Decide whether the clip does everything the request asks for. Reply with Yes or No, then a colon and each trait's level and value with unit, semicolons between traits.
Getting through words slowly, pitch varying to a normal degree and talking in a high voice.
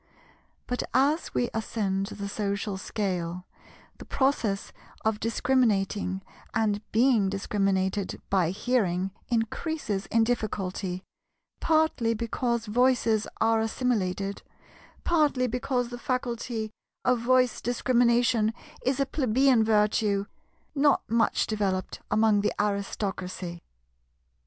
Yes: slow, 100 wpm; average, 3.7 semitones; high, 220 Hz